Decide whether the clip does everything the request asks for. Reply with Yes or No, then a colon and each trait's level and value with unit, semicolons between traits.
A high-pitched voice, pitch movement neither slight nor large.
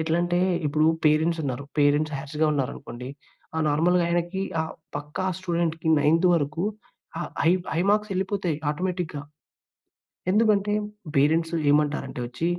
No: medium, 160 Hz; average, 3.2 semitones